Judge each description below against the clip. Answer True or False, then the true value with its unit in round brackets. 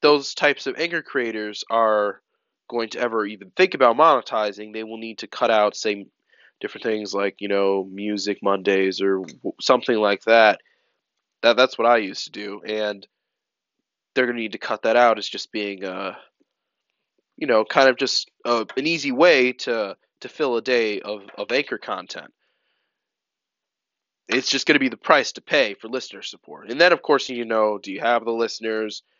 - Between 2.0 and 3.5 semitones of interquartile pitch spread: True (2.8 semitones)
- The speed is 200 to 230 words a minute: False (190 wpm)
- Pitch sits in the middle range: False (110 Hz)